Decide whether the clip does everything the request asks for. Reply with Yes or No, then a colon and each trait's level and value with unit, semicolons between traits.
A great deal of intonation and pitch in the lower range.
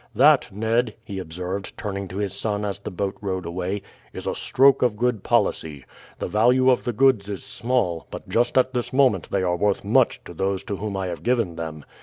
No: average, 4.5 semitones; low, 100 Hz